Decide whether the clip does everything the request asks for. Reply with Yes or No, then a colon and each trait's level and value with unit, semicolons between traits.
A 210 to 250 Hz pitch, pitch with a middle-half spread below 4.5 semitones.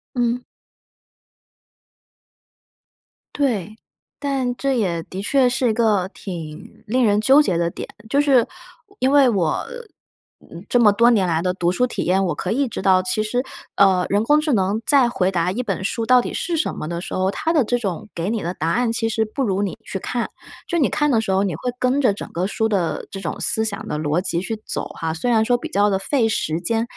No: high, 215 Hz; average, 5.0 semitones